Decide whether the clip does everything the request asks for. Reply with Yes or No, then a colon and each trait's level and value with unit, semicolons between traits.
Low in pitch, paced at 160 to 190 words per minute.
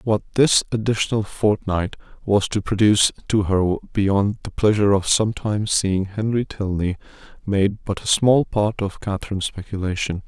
No: low, 100 Hz; average, 145 wpm